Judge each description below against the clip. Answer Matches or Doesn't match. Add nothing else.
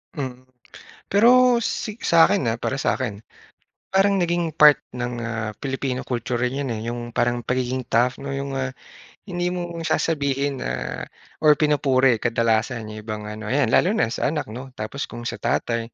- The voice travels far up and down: Doesn't match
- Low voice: Matches